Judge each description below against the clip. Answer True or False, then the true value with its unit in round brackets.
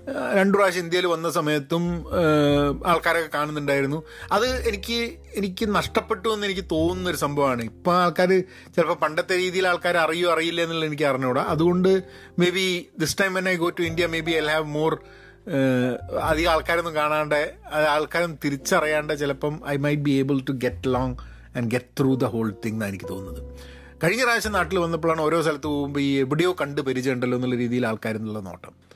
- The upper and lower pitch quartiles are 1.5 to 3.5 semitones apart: False (4.3 semitones)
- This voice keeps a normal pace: False (165 wpm)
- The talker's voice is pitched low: False (155 Hz)